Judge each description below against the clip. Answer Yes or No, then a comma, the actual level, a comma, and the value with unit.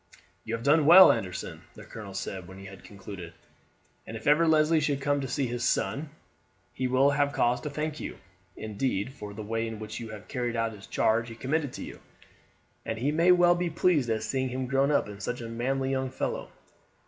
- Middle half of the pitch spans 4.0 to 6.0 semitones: Yes, average, 4.7 semitones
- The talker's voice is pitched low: Yes, low, 130 Hz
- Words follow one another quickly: Yes, fast, 215 wpm